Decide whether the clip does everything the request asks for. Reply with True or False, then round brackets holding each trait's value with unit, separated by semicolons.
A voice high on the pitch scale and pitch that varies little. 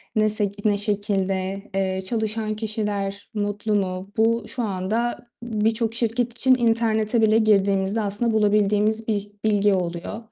True (210 Hz; 2.0 semitones)